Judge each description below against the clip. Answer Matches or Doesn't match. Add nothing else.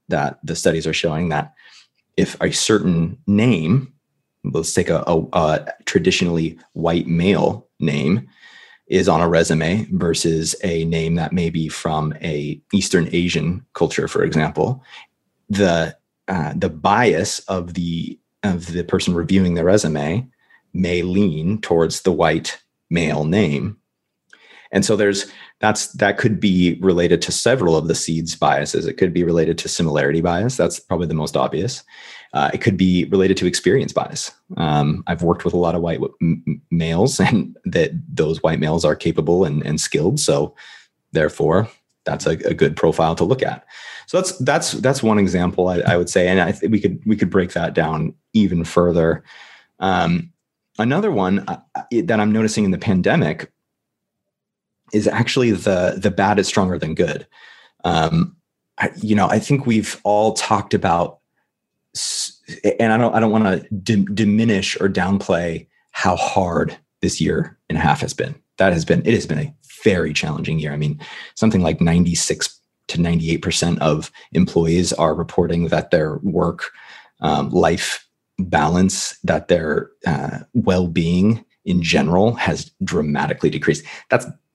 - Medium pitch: Doesn't match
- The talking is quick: Doesn't match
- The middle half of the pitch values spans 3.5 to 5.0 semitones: Matches